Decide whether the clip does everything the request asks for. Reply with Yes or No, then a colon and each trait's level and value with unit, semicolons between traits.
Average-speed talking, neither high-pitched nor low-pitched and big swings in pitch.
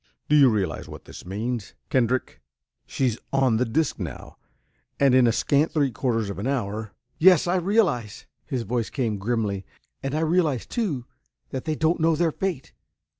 No: average, 175 wpm; low, 130 Hz; wide, 5.7 semitones